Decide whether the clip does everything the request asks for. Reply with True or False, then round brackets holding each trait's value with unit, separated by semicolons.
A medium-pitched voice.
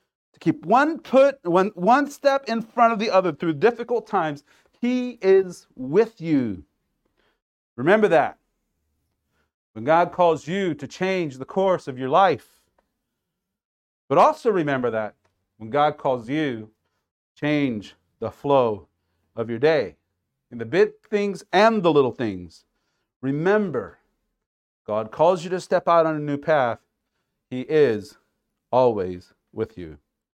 True (155 Hz)